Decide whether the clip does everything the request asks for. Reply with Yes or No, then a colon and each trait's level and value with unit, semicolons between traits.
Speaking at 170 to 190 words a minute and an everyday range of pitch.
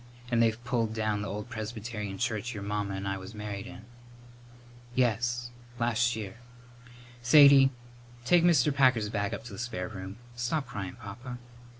No: average, 160 wpm; average, 3.0 semitones